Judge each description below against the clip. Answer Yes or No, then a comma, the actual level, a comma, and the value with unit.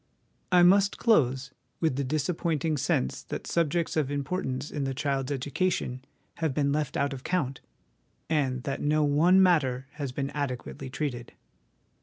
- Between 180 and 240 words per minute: No, average, 150 wpm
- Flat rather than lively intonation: No, average, 3.3 semitones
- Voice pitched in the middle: Yes, medium, 145 Hz